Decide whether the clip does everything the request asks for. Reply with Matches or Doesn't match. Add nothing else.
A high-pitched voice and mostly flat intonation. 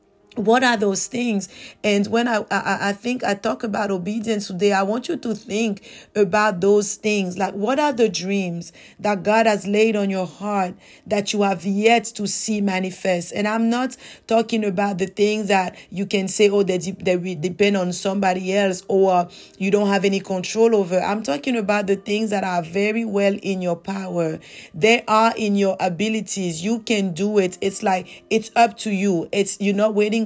Matches